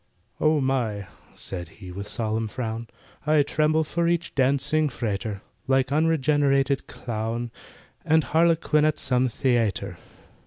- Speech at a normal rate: No, slow, 125 wpm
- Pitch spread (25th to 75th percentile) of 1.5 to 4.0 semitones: No, wide, 5.5 semitones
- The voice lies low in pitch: Yes, low, 130 Hz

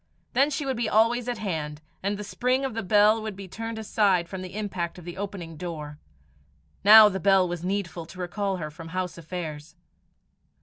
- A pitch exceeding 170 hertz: Yes, high, 190 Hz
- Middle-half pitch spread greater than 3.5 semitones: Yes, average, 4.0 semitones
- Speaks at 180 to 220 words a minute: Yes, average, 200 wpm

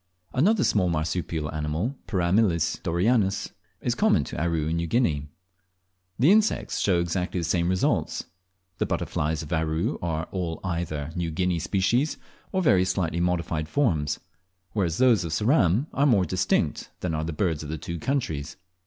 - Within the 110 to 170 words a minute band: Yes, average, 160 wpm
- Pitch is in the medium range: No, very low, 85 Hz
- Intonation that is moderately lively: Yes, average, 3.9 semitones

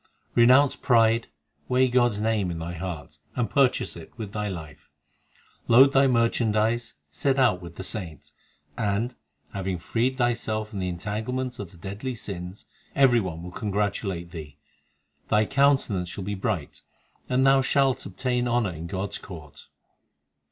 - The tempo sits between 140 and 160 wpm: Yes, average, 155 wpm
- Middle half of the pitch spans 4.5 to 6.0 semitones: Yes, average, 5.2 semitones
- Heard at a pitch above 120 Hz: No, low, 105 Hz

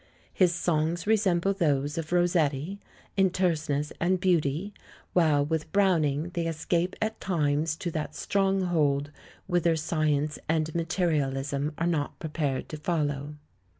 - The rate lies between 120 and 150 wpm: Yes, slow, 135 wpm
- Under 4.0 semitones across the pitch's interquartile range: Yes, average, 3.0 semitones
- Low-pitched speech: No, medium, 160 Hz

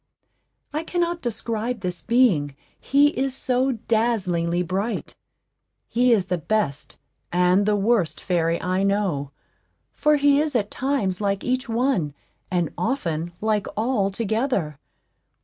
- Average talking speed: No, slow, 130 wpm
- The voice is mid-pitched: No, high, 210 Hz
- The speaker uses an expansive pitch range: Yes, wide, 5.9 semitones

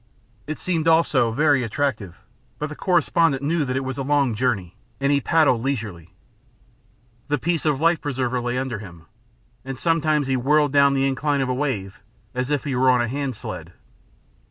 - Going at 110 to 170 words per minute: No, average, 180 wpm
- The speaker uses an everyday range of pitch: Yes, average, 3.1 semitones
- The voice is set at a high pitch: No, low, 135 Hz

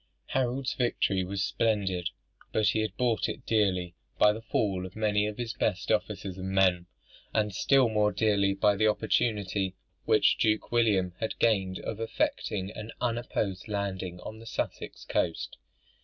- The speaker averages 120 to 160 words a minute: Yes, average, 155 wpm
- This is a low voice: Yes, low, 105 Hz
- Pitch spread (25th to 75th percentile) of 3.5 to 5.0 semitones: No, narrow, 2.6 semitones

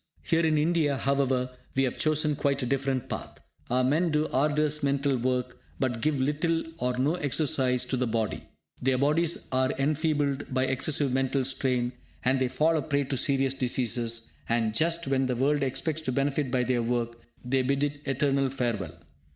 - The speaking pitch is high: No, low, 135 Hz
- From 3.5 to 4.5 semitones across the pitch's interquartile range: No, narrow, 2.6 semitones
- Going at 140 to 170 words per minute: No, average, 180 wpm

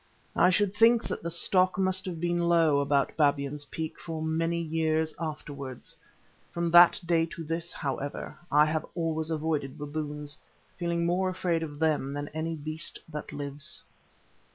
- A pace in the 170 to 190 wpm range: No, average, 155 wpm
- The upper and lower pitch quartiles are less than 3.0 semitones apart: Yes, narrow, 2.5 semitones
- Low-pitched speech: No, medium, 160 Hz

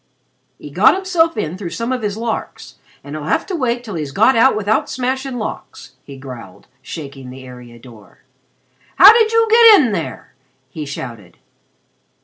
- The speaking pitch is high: Yes, high, 210 Hz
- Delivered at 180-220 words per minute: No, average, 170 wpm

